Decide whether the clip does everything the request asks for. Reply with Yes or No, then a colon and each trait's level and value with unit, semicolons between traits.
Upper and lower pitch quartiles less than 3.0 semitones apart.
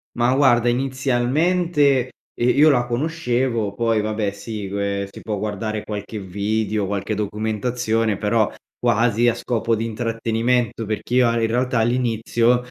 Yes: narrow, 2.5 semitones